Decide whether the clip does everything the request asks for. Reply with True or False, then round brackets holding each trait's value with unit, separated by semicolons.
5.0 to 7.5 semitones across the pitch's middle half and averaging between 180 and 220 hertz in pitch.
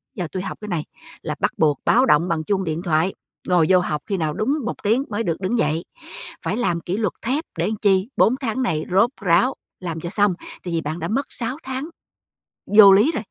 True (5.3 semitones; 190 Hz)